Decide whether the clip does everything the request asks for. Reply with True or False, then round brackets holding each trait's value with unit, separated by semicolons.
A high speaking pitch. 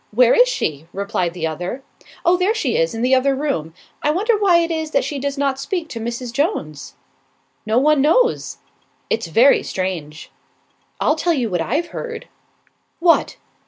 True (270 Hz)